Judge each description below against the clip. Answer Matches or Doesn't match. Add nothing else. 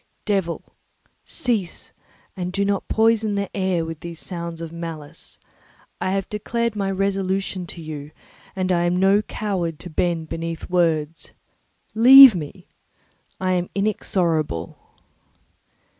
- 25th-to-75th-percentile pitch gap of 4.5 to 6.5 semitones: Doesn't match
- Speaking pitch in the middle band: Matches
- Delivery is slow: Matches